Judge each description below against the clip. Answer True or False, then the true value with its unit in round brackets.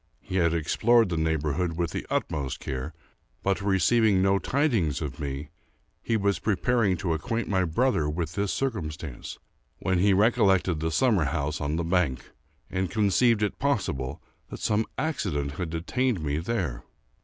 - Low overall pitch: True (90 Hz)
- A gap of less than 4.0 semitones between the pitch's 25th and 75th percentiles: False (5.3 semitones)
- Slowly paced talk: False (155 wpm)